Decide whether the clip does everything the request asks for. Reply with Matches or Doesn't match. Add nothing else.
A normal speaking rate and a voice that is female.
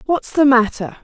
Matches